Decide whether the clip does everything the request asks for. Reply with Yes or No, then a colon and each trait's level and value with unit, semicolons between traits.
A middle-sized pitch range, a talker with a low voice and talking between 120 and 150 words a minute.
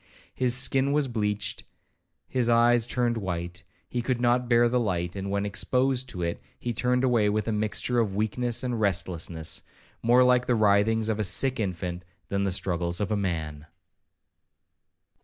No: average, 4.2 semitones; low, 110 Hz; average, 170 wpm